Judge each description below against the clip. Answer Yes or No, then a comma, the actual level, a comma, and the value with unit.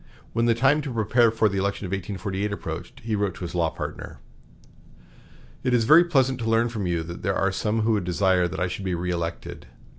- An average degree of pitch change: Yes, average, 4.3 semitones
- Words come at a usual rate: No, fast, 215 wpm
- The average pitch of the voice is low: Yes, low, 100 Hz